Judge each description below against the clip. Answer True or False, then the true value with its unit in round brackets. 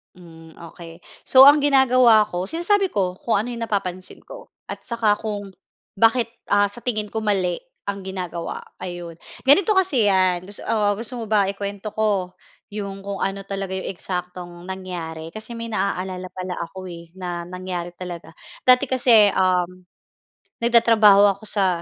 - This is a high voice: True (195 Hz)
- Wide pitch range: False (3.6 semitones)